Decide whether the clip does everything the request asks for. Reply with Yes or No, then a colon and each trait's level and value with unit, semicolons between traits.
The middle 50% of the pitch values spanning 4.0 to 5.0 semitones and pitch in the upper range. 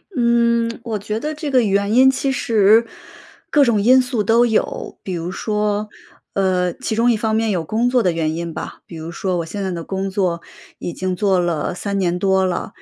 Yes: average, 4.3 semitones; high, 205 Hz